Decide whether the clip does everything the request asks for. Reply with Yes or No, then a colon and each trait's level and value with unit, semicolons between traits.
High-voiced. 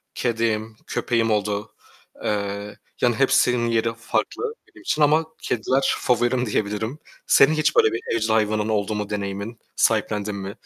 No: low, 110 Hz